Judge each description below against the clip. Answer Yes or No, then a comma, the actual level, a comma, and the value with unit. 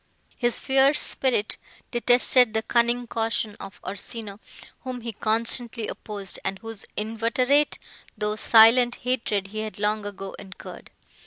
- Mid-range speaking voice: No, high, 225 Hz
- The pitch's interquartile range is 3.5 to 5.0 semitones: No, narrow, 2.5 semitones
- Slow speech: Yes, slow, 130 wpm